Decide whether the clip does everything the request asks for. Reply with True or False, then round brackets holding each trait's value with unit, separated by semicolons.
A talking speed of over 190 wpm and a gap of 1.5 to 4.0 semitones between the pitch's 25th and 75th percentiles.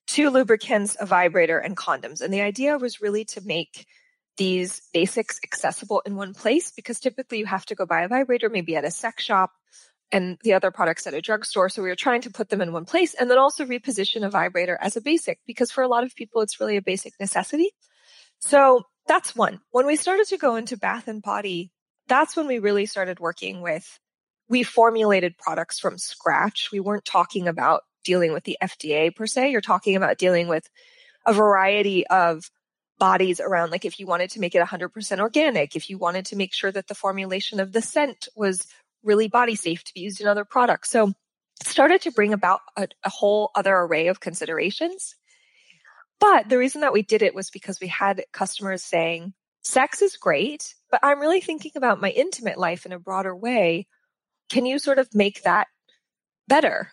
False (200 wpm; 5.2 semitones)